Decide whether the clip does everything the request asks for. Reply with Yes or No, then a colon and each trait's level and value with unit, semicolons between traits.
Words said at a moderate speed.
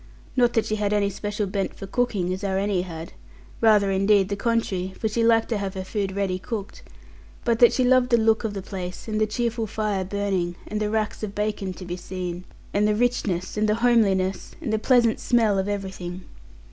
No: fast, 215 wpm